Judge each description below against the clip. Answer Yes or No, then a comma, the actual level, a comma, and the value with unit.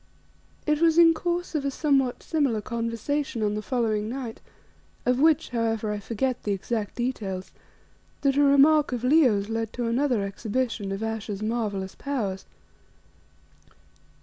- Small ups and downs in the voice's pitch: No, average, 4.7 semitones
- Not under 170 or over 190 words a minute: No, average, 145 wpm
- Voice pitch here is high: Yes, high, 235 Hz